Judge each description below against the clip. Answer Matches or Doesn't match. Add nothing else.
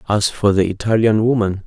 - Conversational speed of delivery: Matches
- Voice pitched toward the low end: Matches